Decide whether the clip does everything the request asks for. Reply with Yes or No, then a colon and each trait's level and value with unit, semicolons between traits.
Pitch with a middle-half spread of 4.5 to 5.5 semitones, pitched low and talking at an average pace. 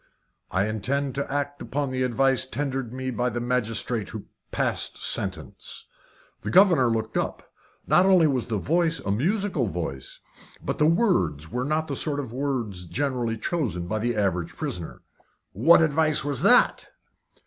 Yes: average, 4.9 semitones; low, 130 Hz; average, 160 wpm